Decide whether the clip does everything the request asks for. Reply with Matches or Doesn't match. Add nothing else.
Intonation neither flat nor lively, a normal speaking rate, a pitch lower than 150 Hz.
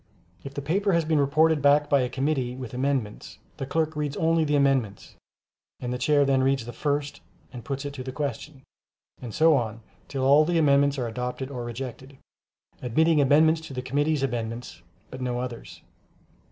Matches